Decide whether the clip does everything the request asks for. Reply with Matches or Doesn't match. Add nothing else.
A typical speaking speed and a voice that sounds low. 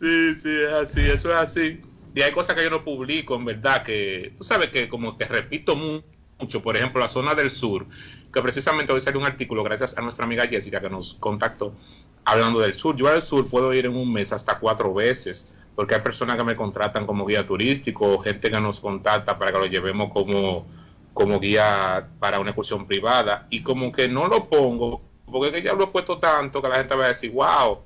Doesn't match